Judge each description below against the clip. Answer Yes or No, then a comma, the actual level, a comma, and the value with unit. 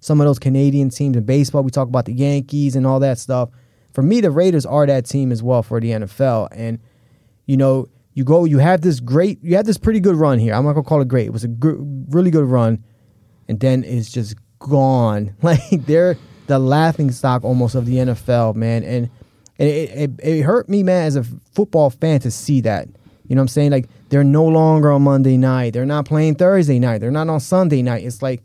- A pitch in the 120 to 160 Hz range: Yes, low, 135 Hz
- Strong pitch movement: No, average, 3.6 semitones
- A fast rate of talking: Yes, fast, 235 wpm